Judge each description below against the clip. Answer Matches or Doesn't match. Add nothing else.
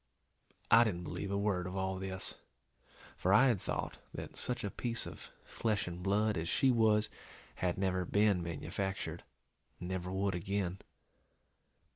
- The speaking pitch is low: Matches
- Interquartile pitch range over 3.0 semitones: Doesn't match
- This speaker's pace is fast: Doesn't match